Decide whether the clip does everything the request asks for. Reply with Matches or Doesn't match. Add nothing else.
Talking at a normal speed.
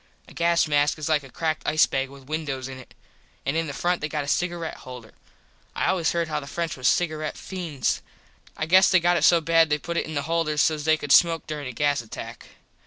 Doesn't match